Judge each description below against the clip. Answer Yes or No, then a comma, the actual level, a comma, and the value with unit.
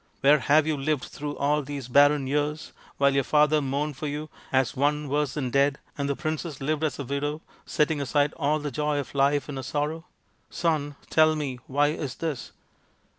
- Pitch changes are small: Yes, narrow, 1.4 semitones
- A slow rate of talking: No, average, 195 wpm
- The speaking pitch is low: No, medium, 145 Hz